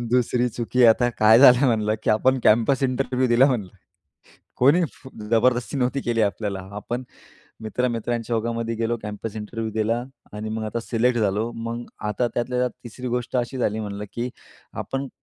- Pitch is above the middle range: No, low, 115 Hz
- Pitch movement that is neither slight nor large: No, narrow, 2.3 semitones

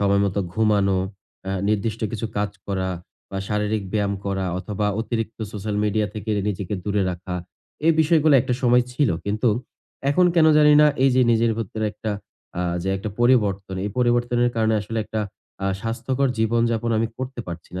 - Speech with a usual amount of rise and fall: Yes, average, 3.0 semitones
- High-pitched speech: No, low, 110 Hz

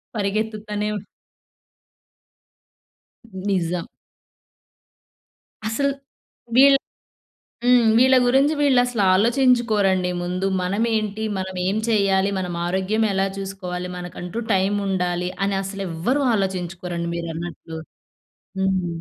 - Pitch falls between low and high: No, high, 195 Hz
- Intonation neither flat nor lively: Yes, average, 3.6 semitones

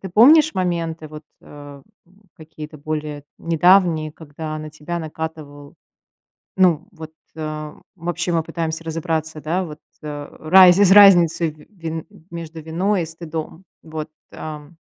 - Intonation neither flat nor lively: No, narrow, 2.2 semitones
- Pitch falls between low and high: Yes, medium, 160 Hz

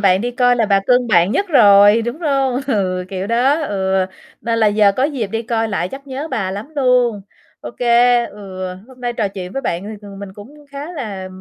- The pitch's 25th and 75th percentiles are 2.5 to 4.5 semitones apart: Yes, average, 4.2 semitones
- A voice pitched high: Yes, high, 230 Hz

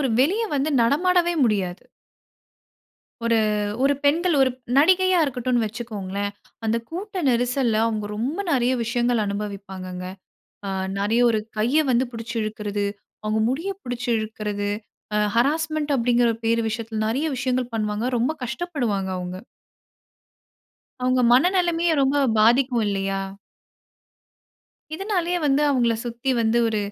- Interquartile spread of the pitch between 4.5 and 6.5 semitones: Yes, average, 4.9 semitones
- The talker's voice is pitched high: Yes, high, 240 Hz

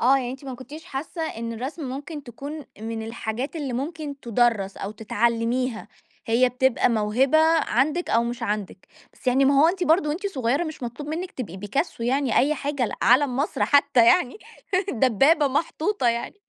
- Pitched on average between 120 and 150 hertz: No, very high, 260 Hz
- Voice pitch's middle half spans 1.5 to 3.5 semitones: No, average, 4.0 semitones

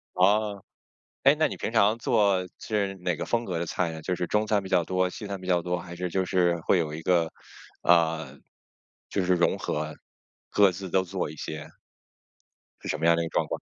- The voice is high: No, very low, 90 Hz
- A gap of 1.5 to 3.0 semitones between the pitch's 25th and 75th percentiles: Yes, average, 2.7 semitones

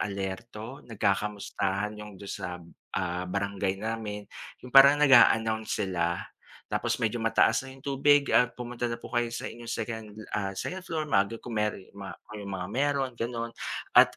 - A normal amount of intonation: Yes, average, 3.5 semitones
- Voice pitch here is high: No, low, 110 Hz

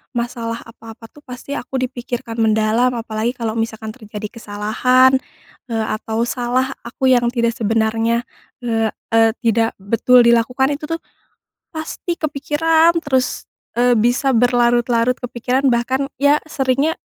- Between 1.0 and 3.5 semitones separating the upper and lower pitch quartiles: Yes, narrow, 2.4 semitones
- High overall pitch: Yes, high, 240 Hz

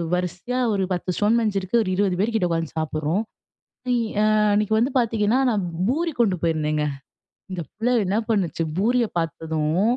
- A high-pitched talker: Yes, high, 195 Hz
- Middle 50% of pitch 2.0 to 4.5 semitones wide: No, average, 5.1 semitones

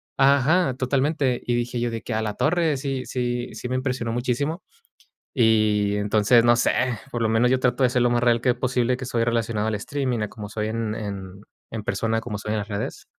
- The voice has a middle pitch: No, low, 120 Hz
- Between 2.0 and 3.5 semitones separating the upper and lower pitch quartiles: Yes, average, 2.7 semitones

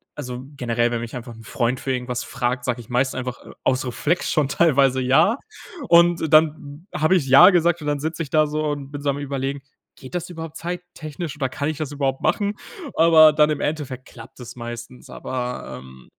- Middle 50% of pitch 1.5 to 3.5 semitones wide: No, average, 3.9 semitones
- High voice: No, medium, 140 Hz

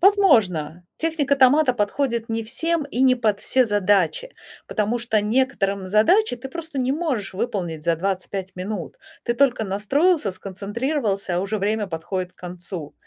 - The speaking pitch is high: Yes, high, 215 Hz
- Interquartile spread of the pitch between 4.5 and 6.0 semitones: Yes, wide, 5.6 semitones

